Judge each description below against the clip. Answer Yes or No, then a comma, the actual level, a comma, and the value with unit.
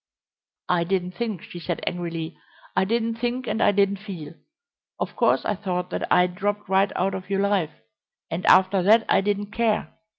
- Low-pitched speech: No, high, 195 Hz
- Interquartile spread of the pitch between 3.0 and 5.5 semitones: No, narrow, 2.6 semitones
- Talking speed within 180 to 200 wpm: Yes, average, 185 wpm